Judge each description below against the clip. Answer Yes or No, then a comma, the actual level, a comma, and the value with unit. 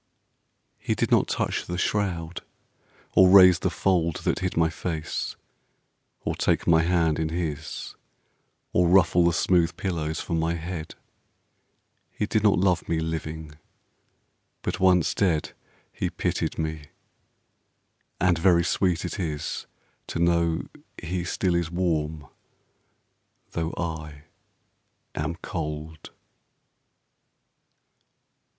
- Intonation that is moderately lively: No, narrow, 2.1 semitones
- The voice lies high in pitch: No, very low, 85 Hz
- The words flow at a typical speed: No, slow, 115 wpm